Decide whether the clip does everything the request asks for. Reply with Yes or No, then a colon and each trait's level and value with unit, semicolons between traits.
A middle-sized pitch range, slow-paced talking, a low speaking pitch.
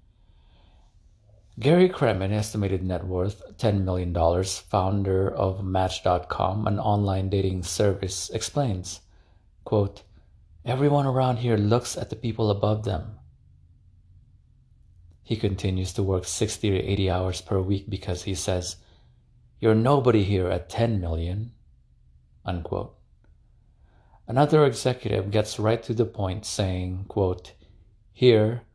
Yes: average, 3.0 semitones; slow, 115 wpm; very low, 95 Hz